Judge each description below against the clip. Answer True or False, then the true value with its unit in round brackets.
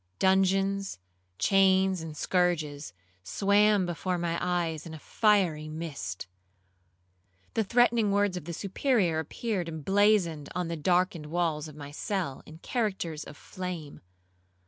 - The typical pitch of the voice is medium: True (180 Hz)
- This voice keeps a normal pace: False (125 wpm)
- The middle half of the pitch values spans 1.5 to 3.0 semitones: False (3.7 semitones)